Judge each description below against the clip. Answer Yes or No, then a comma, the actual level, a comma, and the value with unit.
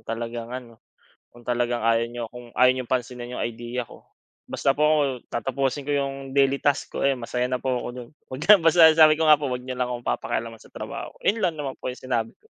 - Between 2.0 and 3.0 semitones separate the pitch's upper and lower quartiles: Yes, narrow, 2.5 semitones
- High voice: No, low, 125 Hz